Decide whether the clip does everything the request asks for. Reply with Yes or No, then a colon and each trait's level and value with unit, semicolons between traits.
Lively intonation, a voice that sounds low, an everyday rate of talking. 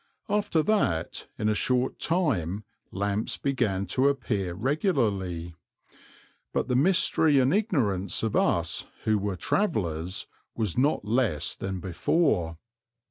No: wide, 7.0 semitones; low, 110 Hz; slow, 120 wpm